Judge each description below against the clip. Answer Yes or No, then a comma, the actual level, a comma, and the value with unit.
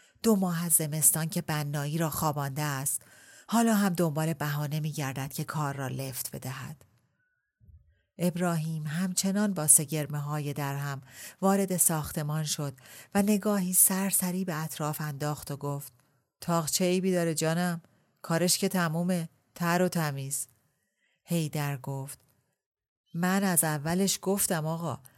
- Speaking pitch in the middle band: Yes, medium, 160 Hz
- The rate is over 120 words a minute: Yes, average, 130 wpm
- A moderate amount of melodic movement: Yes, average, 3.9 semitones